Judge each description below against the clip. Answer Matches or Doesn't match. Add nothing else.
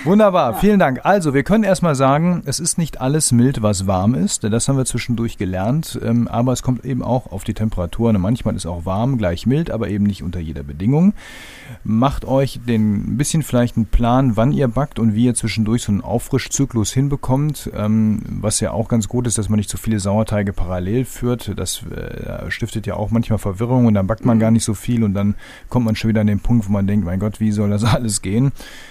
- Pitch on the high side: Doesn't match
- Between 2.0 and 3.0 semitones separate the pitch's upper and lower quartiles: Doesn't match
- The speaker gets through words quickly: Matches